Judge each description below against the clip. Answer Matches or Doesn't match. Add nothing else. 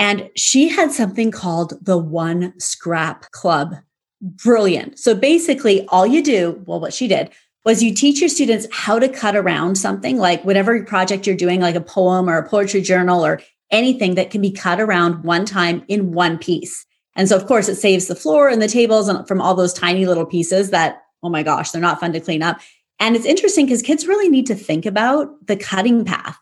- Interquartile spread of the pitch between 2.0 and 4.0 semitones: Doesn't match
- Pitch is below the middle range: Doesn't match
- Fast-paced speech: Matches